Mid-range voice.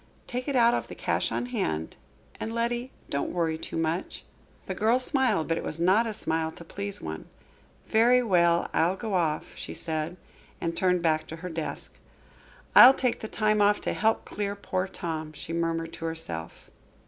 Yes: medium, 180 Hz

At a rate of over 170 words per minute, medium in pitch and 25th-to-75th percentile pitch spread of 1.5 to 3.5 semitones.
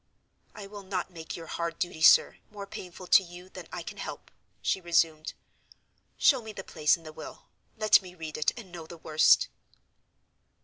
Yes: average, 185 wpm; medium, 175 Hz; average, 3.0 semitones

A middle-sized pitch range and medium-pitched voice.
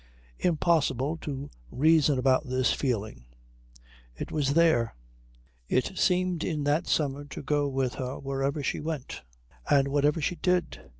Yes: average, 3.1 semitones; medium, 145 Hz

